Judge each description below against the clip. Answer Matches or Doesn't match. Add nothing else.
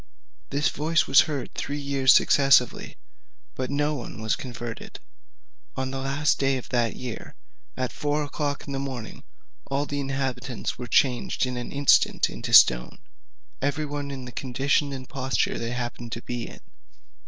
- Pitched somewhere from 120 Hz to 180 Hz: Matches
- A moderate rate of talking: Matches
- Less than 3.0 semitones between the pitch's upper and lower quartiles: Matches